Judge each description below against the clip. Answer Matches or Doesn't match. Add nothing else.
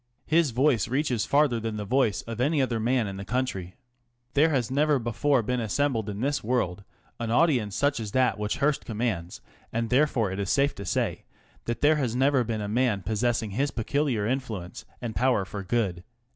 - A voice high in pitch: Doesn't match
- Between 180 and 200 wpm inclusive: Matches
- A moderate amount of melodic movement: Matches